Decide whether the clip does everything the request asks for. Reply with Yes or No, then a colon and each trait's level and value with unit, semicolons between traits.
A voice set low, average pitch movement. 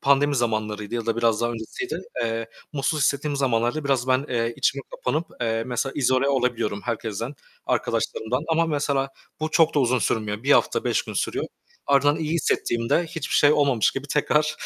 Yes: low, 130 Hz; average, 3.9 semitones